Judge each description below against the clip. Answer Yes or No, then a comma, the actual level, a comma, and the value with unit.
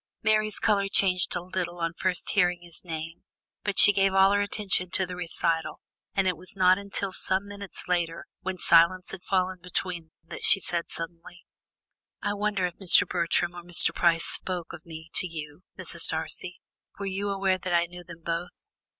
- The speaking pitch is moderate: Yes, medium, 180 Hz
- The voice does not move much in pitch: Yes, narrow, 2.2 semitones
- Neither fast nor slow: Yes, average, 190 wpm